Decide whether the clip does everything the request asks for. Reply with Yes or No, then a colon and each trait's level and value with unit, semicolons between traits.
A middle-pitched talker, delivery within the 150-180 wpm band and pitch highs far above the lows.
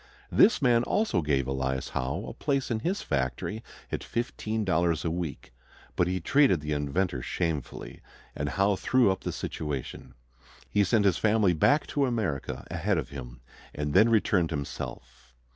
No: very low, 85 Hz; average, 160 wpm; wide, 7.5 semitones